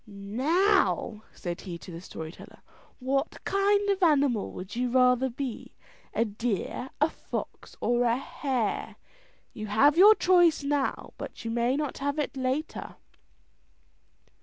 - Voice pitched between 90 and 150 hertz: No, very high, 260 Hz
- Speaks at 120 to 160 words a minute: Yes, average, 140 wpm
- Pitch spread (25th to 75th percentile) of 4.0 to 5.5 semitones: Yes, average, 5.2 semitones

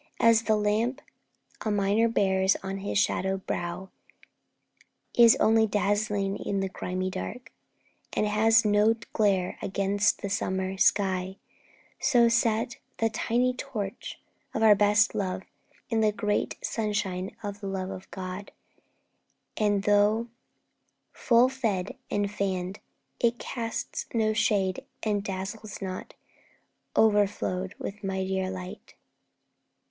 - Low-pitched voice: No, high, 205 Hz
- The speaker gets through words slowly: Yes, slow, 120 wpm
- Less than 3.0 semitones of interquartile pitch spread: Yes, narrow, 2.5 semitones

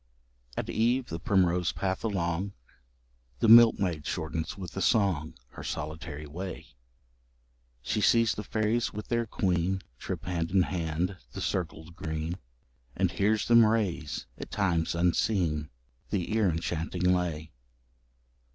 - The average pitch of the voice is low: Yes, very low, 90 Hz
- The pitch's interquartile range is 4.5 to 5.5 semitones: No, average, 3.9 semitones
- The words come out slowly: Yes, slow, 130 wpm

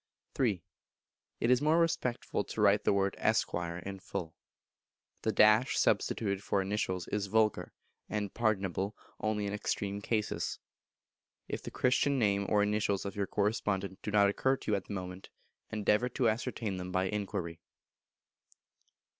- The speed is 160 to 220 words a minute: No, average, 145 wpm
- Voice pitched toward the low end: Yes, low, 105 Hz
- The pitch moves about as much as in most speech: No, narrow, 2.1 semitones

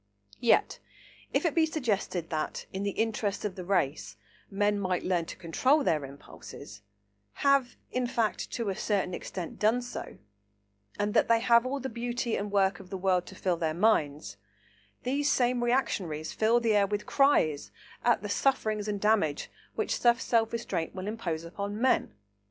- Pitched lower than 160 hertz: No, high, 205 Hz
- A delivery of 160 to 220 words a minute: Yes, average, 170 wpm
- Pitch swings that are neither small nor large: No, wide, 6.1 semitones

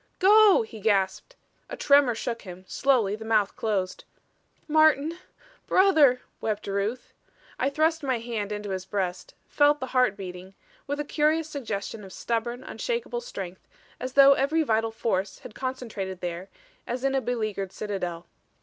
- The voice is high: Yes, high, 230 Hz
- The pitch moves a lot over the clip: Yes, wide, 6.0 semitones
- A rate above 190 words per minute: No, average, 150 wpm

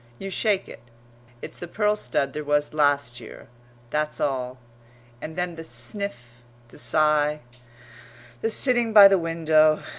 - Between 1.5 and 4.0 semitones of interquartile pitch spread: No, average, 5.3 semitones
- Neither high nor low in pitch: Yes, medium, 155 Hz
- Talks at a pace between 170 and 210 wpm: No, average, 145 wpm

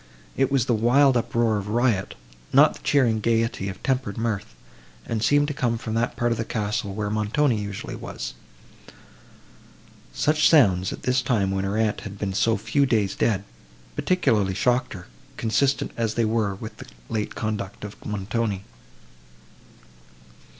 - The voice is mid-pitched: No, low, 110 Hz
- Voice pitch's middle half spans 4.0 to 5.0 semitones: No, average, 3.0 semitones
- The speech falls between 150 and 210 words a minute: Yes, average, 160 wpm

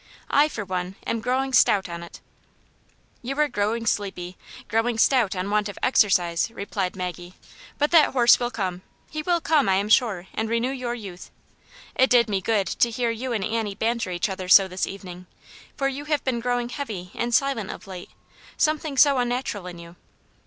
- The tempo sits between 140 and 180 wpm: No, fast, 205 wpm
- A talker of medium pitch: No, high, 225 Hz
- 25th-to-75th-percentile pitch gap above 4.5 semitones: Yes, average, 5.0 semitones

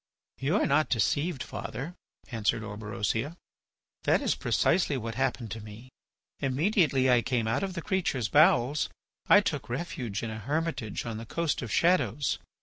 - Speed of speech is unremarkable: Yes, average, 155 wpm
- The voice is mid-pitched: No, low, 130 Hz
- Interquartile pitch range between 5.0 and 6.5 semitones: Yes, wide, 5.6 semitones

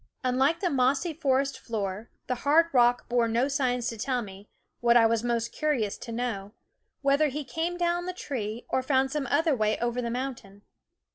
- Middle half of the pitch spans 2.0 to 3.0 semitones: No, average, 3.6 semitones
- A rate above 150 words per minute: Yes, average, 190 wpm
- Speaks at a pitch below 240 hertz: No, very high, 250 Hz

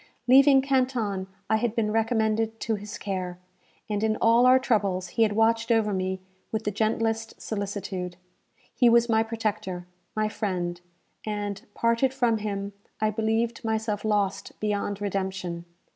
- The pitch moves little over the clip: Yes, narrow, 2.1 semitones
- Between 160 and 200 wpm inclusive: No, average, 145 wpm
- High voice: Yes, high, 215 Hz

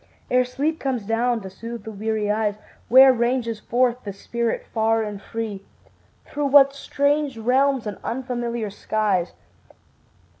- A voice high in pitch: Yes, high, 235 Hz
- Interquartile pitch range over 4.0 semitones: No, average, 3.1 semitones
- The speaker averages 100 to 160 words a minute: Yes, average, 140 wpm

